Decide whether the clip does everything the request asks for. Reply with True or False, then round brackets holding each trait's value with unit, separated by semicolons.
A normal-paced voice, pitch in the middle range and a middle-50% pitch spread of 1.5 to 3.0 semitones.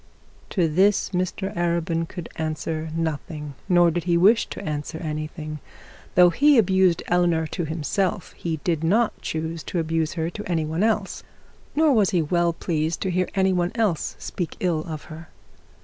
True (165 wpm; 170 Hz; 2.7 semitones)